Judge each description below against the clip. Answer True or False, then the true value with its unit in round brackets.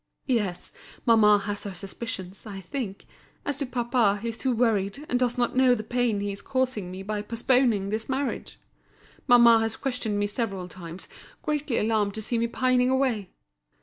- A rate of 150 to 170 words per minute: False (180 wpm)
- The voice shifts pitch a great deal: False (3.7 semitones)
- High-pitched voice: True (225 Hz)